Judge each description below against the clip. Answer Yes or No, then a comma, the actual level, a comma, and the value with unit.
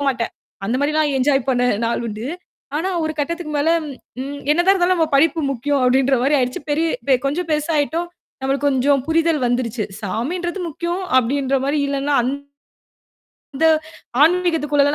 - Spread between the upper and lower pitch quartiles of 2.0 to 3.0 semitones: No, average, 3.6 semitones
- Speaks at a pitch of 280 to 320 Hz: Yes, very high, 285 Hz